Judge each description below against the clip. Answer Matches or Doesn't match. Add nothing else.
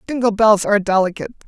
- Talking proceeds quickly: Doesn't match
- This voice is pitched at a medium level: Doesn't match